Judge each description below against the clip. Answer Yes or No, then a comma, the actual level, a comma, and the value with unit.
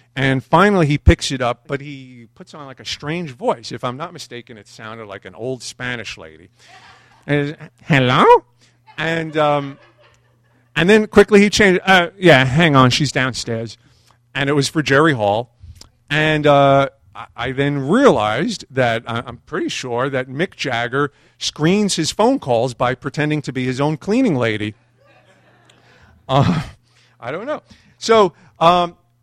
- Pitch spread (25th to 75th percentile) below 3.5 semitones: No, average, 4.8 semitones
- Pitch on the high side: No, low, 135 Hz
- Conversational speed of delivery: Yes, average, 160 wpm